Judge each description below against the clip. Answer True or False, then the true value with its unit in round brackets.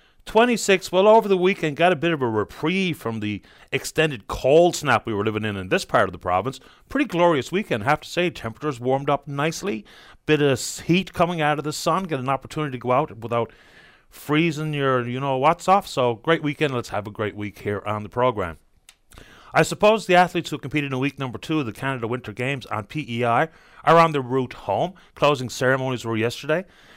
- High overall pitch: False (140 Hz)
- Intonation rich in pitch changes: True (5.8 semitones)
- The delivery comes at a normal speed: False (215 wpm)